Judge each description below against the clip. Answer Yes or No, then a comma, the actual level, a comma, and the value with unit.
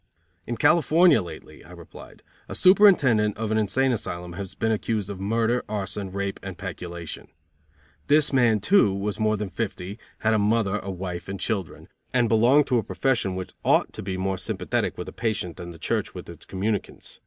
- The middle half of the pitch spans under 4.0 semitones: Yes, average, 3.5 semitones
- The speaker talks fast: No, average, 190 wpm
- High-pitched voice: No, low, 105 Hz